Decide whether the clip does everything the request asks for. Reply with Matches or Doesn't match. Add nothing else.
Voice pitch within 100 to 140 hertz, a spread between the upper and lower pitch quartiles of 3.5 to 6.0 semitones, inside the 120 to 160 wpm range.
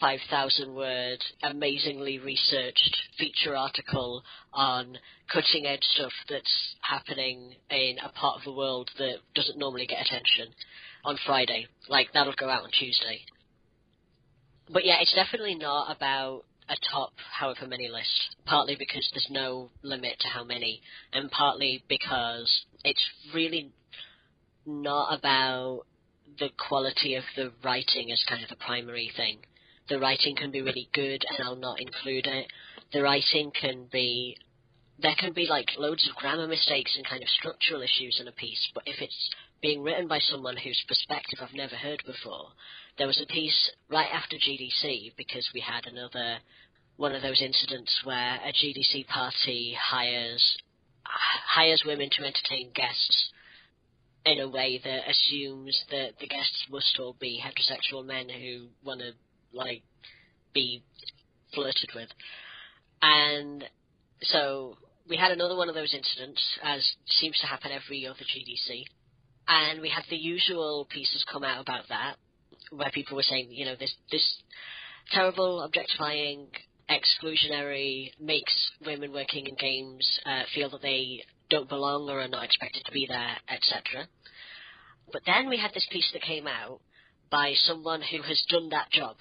Doesn't match